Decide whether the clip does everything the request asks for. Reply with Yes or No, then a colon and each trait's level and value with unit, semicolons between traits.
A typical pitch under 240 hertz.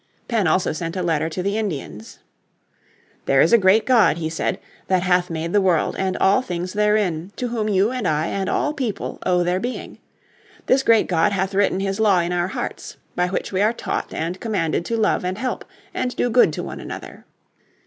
Yes: high, 190 Hz